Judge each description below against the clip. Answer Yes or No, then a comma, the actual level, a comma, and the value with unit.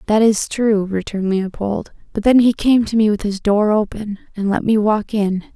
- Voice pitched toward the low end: No, high, 210 Hz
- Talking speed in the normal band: No, fast, 215 wpm